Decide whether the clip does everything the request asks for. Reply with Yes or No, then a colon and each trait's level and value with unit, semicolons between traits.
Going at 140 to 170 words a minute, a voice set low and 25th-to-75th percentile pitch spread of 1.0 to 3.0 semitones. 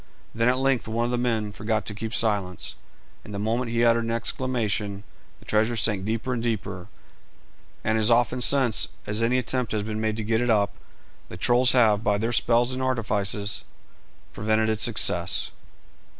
No: average, 180 wpm; low, 110 Hz; narrow, 2.4 semitones